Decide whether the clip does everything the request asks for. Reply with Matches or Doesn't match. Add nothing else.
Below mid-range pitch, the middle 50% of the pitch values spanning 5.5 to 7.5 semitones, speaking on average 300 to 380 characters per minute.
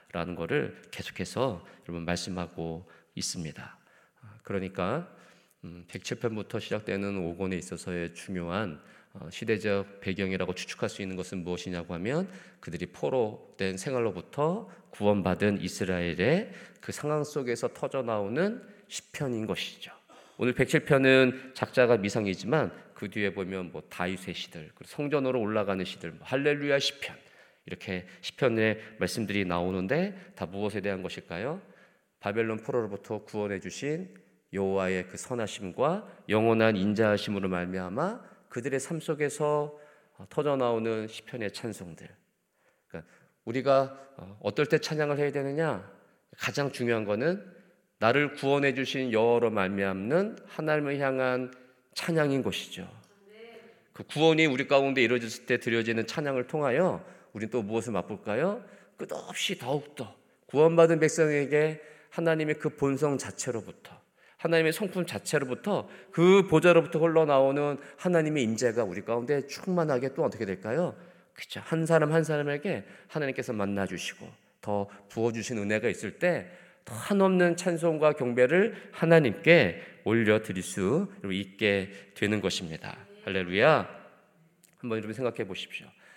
Matches